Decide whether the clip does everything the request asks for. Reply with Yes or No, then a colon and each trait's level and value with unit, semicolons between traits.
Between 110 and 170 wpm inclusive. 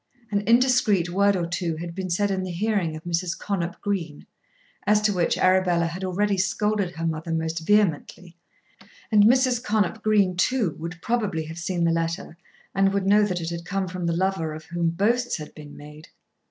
No: average, 195 wpm